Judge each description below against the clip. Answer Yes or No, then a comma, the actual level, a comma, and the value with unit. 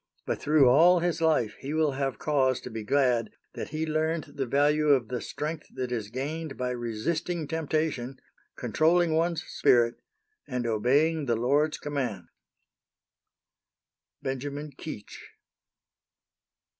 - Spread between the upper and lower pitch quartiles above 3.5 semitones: Yes, average, 4.0 semitones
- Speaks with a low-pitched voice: No, medium, 145 Hz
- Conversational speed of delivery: No, slow, 130 wpm